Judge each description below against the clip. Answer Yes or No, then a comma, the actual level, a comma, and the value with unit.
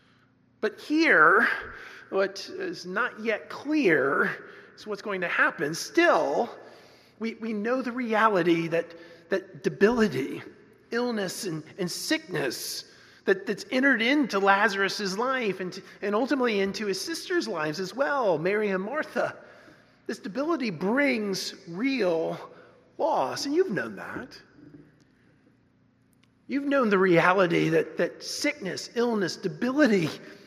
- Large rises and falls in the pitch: Yes, wide, 6.5 semitones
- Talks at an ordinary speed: No, slow, 120 wpm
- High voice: Yes, high, 210 Hz